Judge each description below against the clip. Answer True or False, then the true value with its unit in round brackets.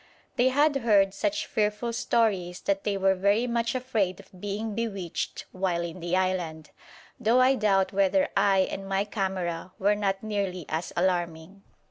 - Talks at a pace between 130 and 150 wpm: False (160 wpm)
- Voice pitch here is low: False (195 Hz)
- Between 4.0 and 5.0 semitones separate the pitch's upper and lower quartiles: False (3.2 semitones)